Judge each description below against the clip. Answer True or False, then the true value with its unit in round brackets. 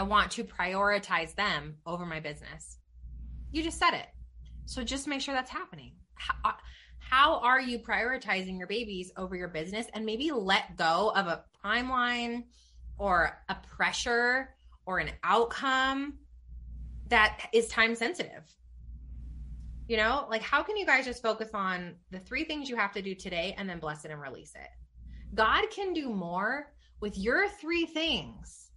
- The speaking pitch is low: False (210 Hz)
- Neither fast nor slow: True (165 wpm)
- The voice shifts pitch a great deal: True (7.9 semitones)